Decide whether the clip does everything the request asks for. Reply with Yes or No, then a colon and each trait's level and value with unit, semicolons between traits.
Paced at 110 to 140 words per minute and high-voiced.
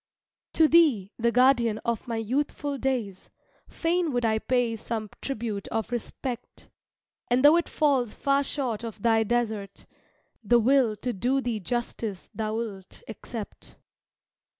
Yes: slow, 135 wpm; high, 235 Hz